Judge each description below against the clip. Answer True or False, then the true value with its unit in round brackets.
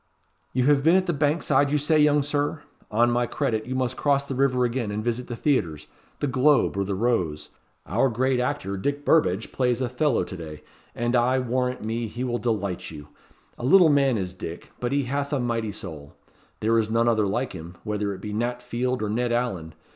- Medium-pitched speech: False (120 Hz)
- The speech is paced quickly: True (210 wpm)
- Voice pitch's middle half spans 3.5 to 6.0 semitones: True (4.3 semitones)